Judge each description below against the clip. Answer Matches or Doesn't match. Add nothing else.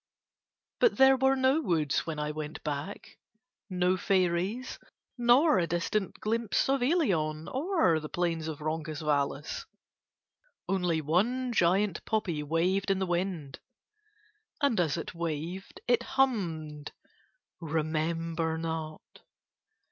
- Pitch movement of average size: Doesn't match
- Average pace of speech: Doesn't match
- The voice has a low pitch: Doesn't match